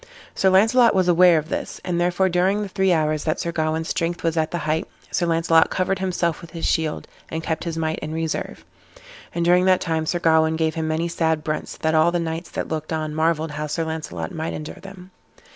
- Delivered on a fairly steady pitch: Yes, narrow, 2.0 semitones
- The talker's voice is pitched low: No, medium, 165 Hz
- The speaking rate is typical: No, fast, 225 wpm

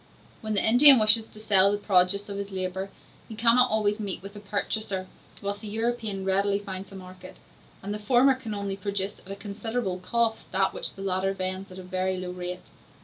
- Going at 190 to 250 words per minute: Yes, fast, 205 wpm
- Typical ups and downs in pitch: No, narrow, 2.3 semitones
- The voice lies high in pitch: Yes, high, 200 Hz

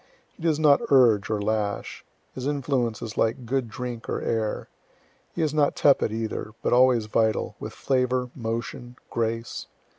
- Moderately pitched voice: No, low, 120 Hz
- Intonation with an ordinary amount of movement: Yes, average, 3.1 semitones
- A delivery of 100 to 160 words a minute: Yes, average, 155 wpm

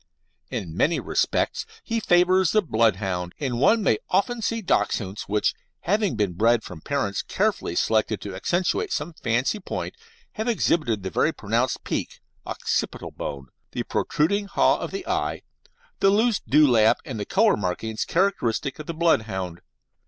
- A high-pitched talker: No, medium, 140 Hz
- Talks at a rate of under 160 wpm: Yes, average, 150 wpm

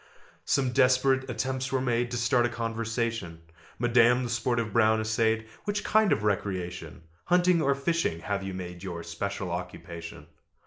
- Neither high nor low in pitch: No, low, 115 Hz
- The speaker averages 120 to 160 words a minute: Yes, average, 150 wpm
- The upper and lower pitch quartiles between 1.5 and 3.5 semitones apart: No, average, 4.8 semitones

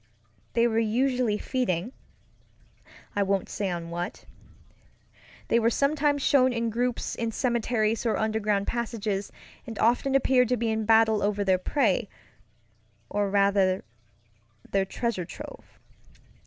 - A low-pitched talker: No, high, 225 Hz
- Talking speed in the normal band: No, slow, 120 wpm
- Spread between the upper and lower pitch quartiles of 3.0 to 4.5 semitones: Yes, average, 3.3 semitones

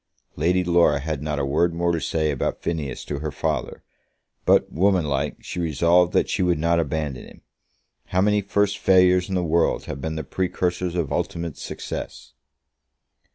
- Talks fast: No, average, 170 wpm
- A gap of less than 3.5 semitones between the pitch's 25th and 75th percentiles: Yes, average, 2.9 semitones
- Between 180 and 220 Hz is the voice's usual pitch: No, very low, 85 Hz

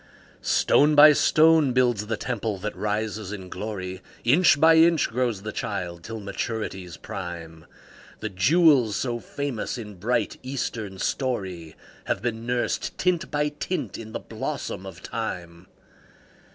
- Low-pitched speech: Yes, low, 110 Hz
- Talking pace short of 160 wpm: Yes, average, 140 wpm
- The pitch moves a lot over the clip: Yes, wide, 6.0 semitones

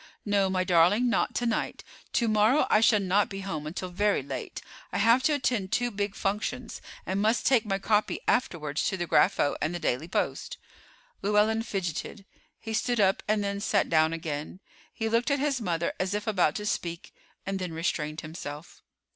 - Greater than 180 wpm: Yes, average, 190 wpm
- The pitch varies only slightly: No, average, 4.3 semitones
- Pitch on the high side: Yes, high, 200 Hz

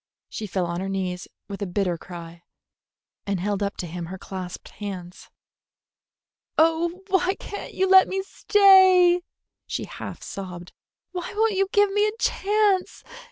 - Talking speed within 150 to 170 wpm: Yes, average, 155 wpm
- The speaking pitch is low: No, high, 210 Hz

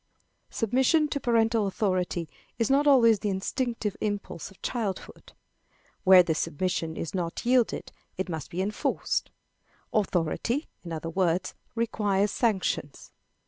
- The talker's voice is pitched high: Yes, high, 200 Hz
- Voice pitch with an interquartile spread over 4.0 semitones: Yes, average, 4.6 semitones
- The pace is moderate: No, slow, 125 wpm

